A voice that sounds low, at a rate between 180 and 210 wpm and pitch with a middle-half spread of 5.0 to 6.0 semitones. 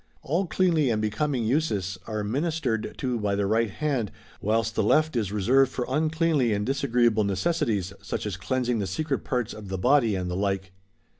Yes: low, 115 Hz; average, 190 wpm; wide, 5.4 semitones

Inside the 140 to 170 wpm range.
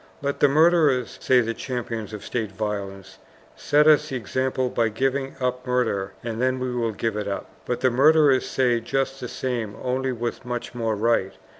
No: average, 185 wpm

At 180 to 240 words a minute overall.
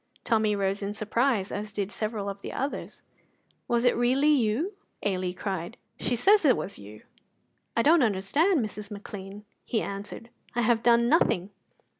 No: average, 160 wpm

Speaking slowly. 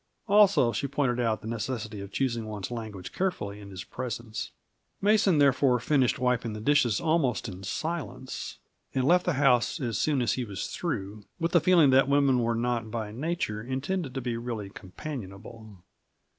No: average, 170 wpm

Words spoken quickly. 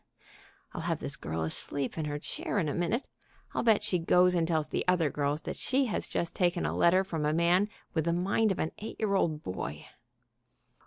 Yes: fast, 220 wpm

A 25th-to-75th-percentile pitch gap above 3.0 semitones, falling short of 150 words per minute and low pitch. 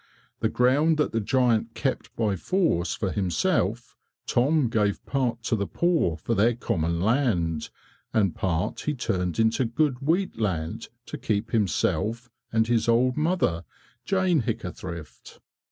Yes: wide, 5.6 semitones; average, 140 wpm; low, 115 Hz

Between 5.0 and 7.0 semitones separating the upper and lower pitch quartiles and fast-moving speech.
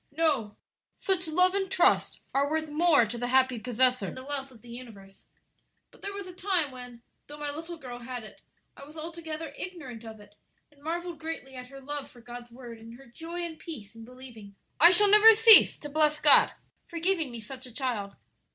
Yes: average, 5.3 semitones; fast, 210 wpm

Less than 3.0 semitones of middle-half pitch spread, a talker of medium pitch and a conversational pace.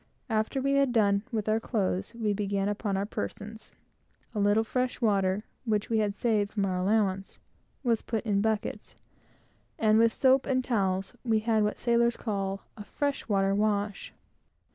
No: narrow, 2.4 semitones; high, 215 Hz; average, 170 wpm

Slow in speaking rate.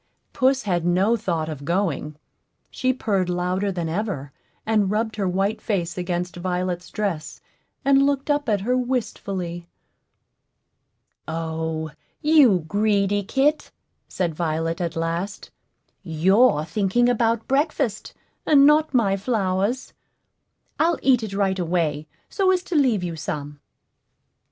Yes: slow, 125 wpm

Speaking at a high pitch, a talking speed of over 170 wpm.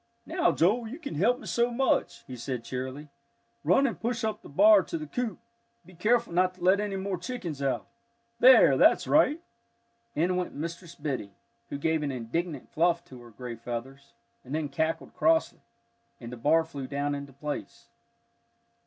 No: medium, 165 Hz; average, 180 wpm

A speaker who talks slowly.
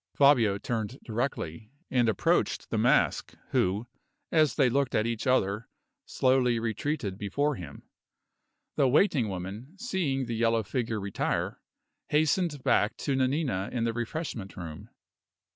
Yes: slow, 130 wpm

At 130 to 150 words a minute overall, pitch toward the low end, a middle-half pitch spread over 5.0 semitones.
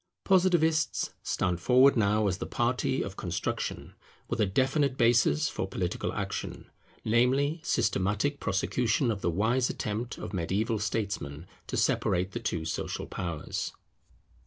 Yes: slow, 135 wpm; low, 110 Hz; wide, 5.5 semitones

